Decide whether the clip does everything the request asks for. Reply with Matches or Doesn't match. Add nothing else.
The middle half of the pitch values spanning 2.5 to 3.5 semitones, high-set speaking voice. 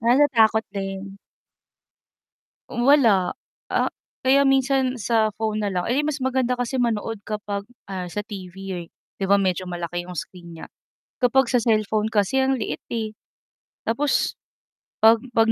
Doesn't match